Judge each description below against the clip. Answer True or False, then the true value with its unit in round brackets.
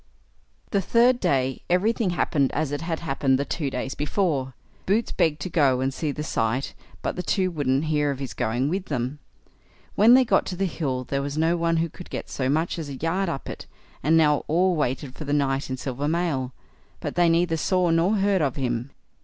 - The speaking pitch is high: False (150 Hz)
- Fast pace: True (215 wpm)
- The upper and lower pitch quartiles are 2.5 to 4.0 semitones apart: False (4.5 semitones)